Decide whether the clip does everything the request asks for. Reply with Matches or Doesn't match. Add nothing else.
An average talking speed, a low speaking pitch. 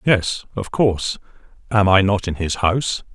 Matches